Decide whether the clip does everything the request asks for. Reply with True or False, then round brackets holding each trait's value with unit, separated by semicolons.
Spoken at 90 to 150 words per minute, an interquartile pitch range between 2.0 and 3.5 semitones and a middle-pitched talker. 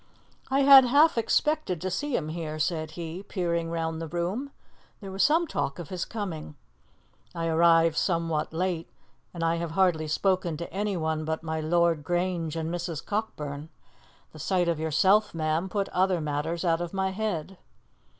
False (170 wpm; 3.0 semitones; 170 Hz)